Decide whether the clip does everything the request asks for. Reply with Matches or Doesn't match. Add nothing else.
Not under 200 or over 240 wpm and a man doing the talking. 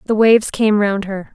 Doesn't match